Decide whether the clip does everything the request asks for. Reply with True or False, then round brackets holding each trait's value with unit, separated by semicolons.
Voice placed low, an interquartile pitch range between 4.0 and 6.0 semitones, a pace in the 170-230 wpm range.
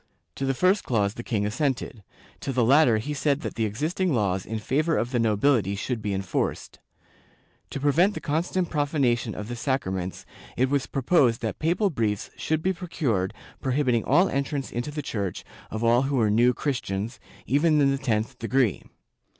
True (130 Hz; 5.0 semitones; 180 wpm)